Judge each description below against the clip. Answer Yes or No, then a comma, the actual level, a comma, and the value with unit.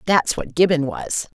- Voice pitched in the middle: Yes, medium, 160 Hz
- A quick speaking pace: No, average, 170 wpm